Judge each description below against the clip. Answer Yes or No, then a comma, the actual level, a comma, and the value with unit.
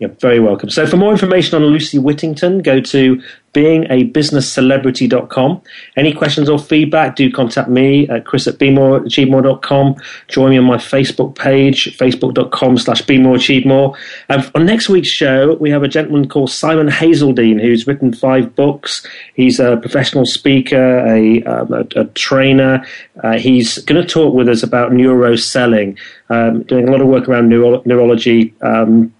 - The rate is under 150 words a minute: No, average, 165 wpm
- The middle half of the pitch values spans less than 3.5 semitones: Yes, narrow, 2.6 semitones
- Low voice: Yes, low, 130 Hz